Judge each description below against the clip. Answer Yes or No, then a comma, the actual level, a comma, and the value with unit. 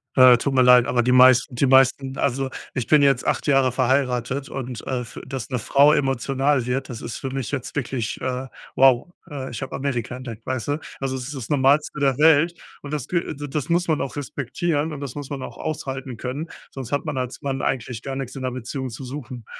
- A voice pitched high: No, low, 135 Hz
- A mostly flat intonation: Yes, narrow, 2.1 semitones